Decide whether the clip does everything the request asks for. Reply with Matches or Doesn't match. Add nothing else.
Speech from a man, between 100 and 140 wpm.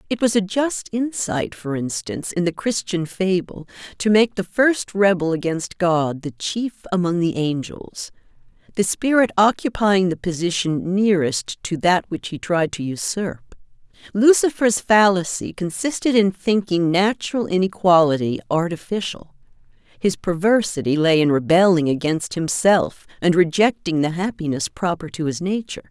Doesn't match